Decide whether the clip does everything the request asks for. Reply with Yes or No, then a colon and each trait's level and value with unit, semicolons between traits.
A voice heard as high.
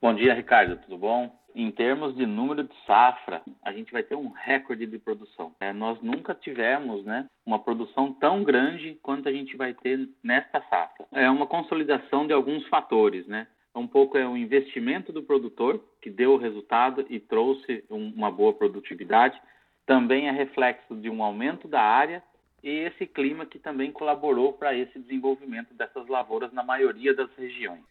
No: medium, 140 Hz